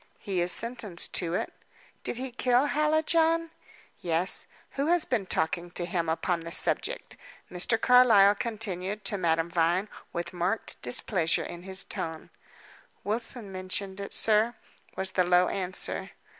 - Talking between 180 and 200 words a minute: No, average, 145 wpm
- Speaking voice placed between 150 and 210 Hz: Yes, high, 190 Hz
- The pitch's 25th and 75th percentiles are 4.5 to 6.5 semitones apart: Yes, average, 5.0 semitones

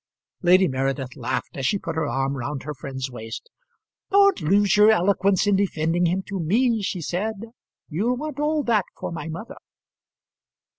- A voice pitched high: No, medium, 180 Hz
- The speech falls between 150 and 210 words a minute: Yes, average, 165 wpm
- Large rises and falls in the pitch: Yes, wide, 6.6 semitones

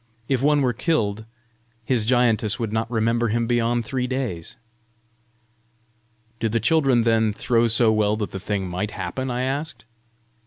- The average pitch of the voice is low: Yes, low, 115 Hz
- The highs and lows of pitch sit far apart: No, narrow, 2.6 semitones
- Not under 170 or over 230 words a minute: No, average, 155 wpm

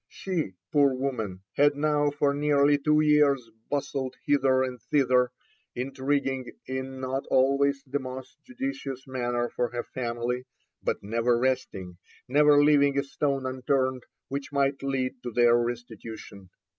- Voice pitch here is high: No, low, 130 Hz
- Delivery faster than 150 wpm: No, slow, 135 wpm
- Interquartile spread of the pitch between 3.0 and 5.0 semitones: No, narrow, 2.4 semitones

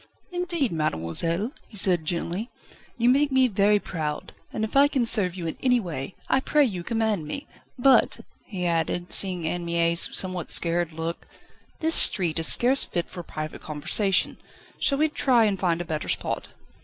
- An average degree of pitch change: No, wide, 6.4 semitones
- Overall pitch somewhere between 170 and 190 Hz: Yes, medium, 185 Hz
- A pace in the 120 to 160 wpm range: No, average, 170 wpm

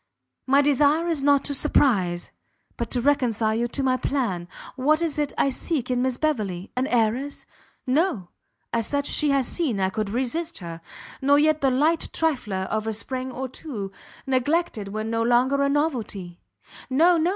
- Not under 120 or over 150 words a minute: No, average, 175 wpm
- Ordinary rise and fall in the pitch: Yes, average, 4.6 semitones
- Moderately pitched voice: No, very high, 260 Hz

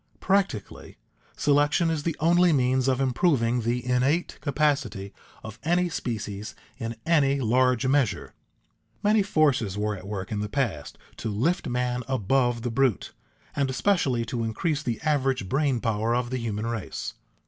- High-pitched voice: No, low, 125 Hz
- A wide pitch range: No, average, 4.3 semitones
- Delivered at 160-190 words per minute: No, average, 150 wpm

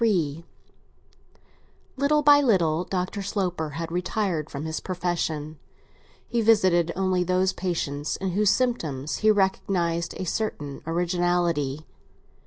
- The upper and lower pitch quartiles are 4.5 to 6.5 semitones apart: No, average, 3.5 semitones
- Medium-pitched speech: Yes, medium, 180 Hz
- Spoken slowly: Yes, slow, 115 wpm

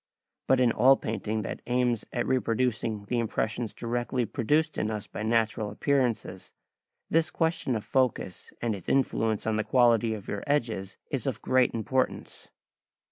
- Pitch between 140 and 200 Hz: No, low, 115 Hz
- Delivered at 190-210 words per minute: No, average, 155 wpm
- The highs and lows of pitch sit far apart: No, average, 3.0 semitones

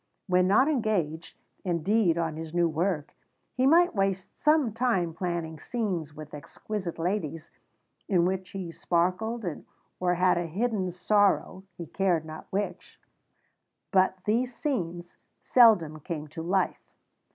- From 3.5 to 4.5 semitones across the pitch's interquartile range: Yes, average, 4.0 semitones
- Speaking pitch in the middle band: Yes, medium, 180 Hz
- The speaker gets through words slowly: Yes, slow, 130 wpm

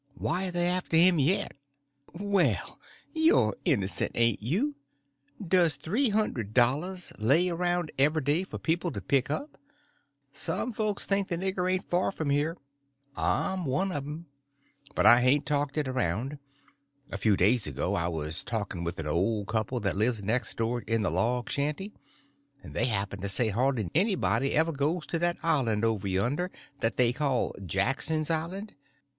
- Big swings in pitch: Yes, wide, 7.6 semitones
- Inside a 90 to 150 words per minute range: No, average, 165 wpm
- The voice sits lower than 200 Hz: Yes, medium, 140 Hz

